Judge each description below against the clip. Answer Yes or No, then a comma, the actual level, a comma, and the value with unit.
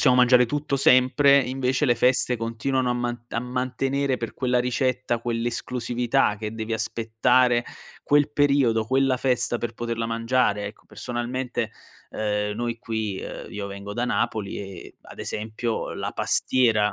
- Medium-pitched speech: No, low, 120 Hz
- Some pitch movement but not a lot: No, narrow, 2.3 semitones